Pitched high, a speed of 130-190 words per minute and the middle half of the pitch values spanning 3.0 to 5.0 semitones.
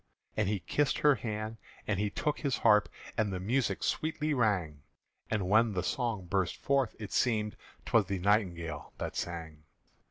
No: low, 105 Hz; average, 165 wpm; average, 4.3 semitones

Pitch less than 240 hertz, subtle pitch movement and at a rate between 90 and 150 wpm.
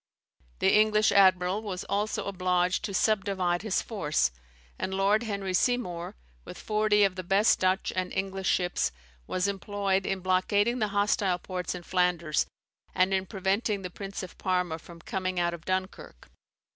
No: high, 190 Hz; narrow, 2.0 semitones; average, 160 wpm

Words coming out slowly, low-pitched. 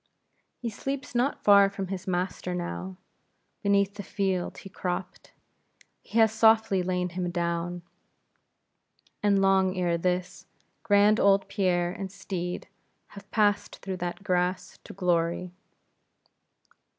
No: slow, 125 wpm; high, 190 Hz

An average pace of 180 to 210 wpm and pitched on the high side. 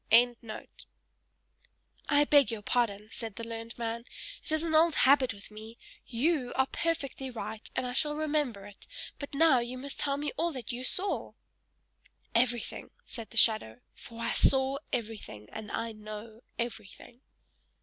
No: average, 150 wpm; high, 240 Hz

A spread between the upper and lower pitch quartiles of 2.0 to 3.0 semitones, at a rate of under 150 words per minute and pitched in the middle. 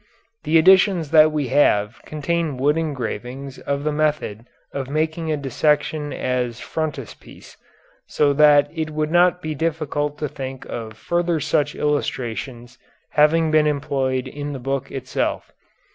Yes: average, 2.7 semitones; average, 140 wpm; medium, 145 Hz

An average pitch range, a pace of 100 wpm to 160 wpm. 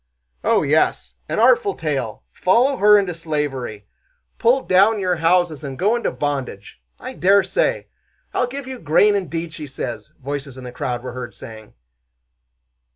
No: wide, 7.5 semitones; average, 155 wpm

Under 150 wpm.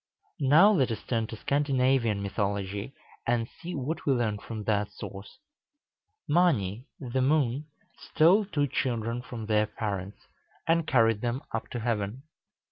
Yes: average, 140 wpm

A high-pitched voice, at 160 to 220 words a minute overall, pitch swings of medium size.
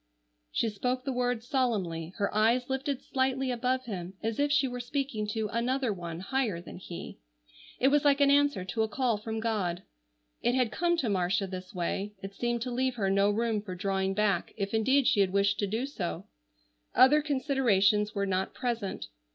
Yes: high, 225 Hz; average, 190 wpm; average, 4.7 semitones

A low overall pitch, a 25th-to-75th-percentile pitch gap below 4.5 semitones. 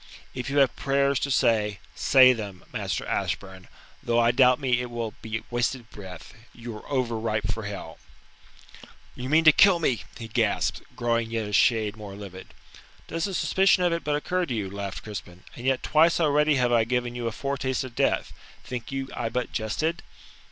Yes: low, 120 Hz; average, 3.9 semitones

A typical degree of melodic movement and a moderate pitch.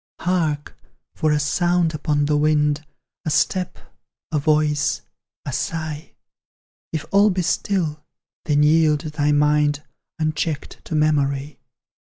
No: narrow, 1.5 semitones; medium, 150 Hz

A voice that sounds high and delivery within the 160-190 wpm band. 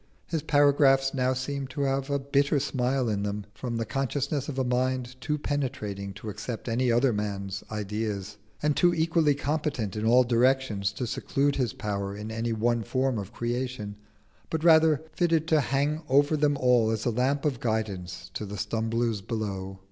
No: low, 125 Hz; average, 180 wpm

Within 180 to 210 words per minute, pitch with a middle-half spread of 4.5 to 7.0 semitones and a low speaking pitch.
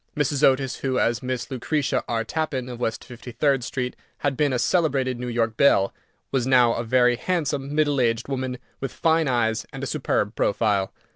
No: average, 185 wpm; average, 2.8 semitones; low, 130 Hz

